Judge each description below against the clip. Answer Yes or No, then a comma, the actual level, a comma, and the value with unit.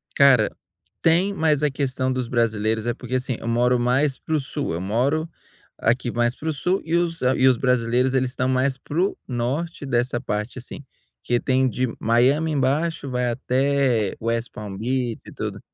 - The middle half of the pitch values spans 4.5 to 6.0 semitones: No, average, 2.9 semitones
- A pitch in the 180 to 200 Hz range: No, low, 130 Hz